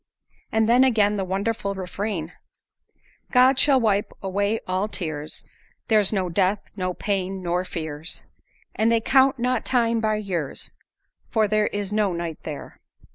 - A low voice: No, high, 205 Hz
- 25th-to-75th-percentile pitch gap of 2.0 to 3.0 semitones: No, average, 3.4 semitones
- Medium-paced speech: Yes, average, 145 wpm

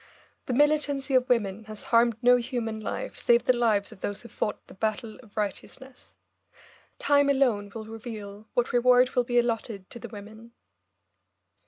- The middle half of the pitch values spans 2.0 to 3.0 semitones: Yes, narrow, 2.6 semitones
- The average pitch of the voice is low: No, high, 235 Hz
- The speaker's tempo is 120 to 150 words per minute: No, average, 165 wpm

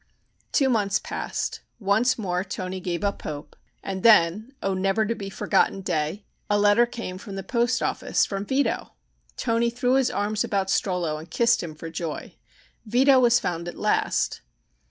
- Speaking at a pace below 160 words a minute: No, average, 170 wpm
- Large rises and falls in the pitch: No, average, 4.3 semitones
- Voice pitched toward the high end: Yes, high, 200 Hz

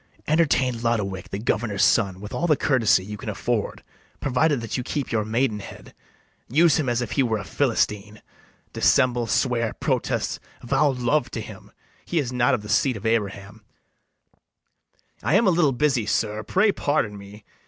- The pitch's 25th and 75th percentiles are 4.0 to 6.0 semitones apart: Yes, average, 4.6 semitones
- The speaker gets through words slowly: No, average, 180 wpm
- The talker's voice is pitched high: No, low, 120 Hz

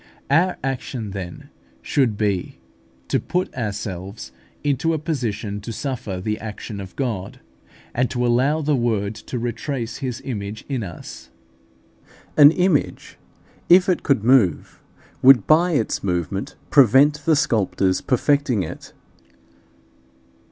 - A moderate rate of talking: No, slow, 125 wpm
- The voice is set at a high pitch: No, low, 120 Hz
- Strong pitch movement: Yes, wide, 5.7 semitones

